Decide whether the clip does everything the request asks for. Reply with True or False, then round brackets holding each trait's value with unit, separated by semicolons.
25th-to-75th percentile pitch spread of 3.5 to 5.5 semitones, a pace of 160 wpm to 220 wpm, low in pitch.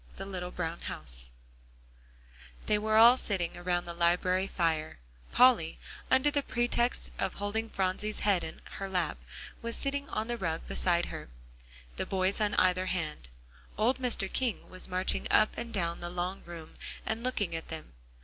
False (4.3 semitones; 170 wpm; 185 Hz)